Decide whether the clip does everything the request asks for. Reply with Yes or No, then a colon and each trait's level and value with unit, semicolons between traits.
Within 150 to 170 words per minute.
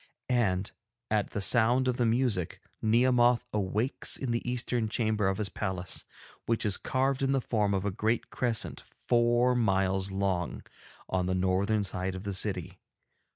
Yes: average, 160 wpm